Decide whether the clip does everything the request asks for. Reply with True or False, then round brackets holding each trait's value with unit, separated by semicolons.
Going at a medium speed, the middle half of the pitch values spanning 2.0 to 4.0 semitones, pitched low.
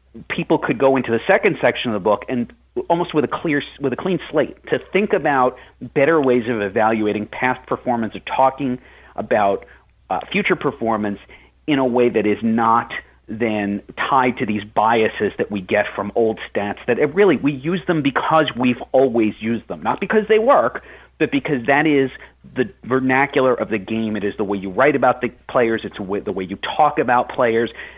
False (195 wpm; 4.6 semitones; 125 Hz)